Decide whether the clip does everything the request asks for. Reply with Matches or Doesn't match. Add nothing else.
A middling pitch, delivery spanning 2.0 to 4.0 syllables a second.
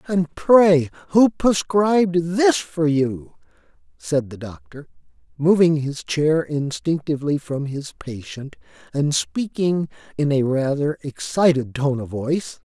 Matches